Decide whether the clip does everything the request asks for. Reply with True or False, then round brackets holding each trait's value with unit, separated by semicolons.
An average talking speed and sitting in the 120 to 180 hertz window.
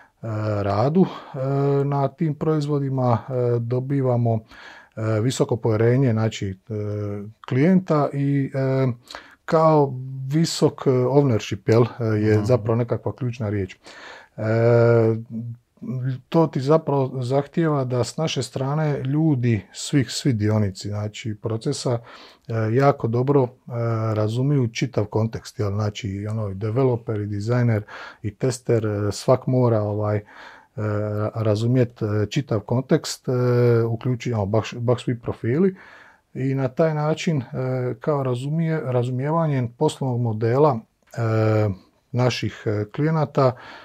False (90 wpm; 125 Hz)